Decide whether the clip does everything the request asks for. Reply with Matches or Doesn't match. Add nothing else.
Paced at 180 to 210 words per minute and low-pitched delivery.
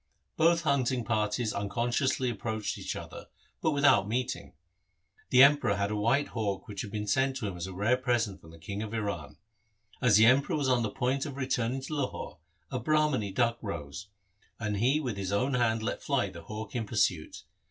Matches